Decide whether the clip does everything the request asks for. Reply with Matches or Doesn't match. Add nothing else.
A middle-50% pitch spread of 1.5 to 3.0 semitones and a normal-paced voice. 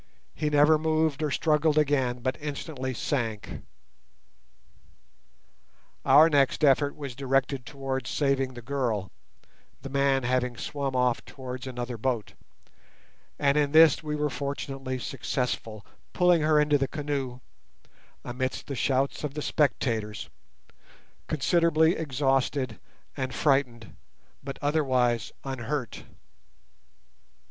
Doesn't match